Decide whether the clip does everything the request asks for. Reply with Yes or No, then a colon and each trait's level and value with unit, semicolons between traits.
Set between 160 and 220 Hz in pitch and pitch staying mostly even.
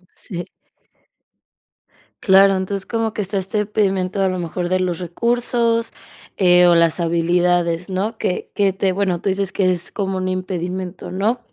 Yes: medium, 185 Hz; narrow, 2.0 semitones